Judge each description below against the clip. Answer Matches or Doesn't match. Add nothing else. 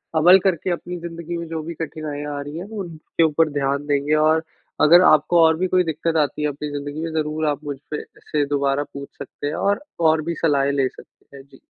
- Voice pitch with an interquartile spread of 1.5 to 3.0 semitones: Matches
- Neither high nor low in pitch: Matches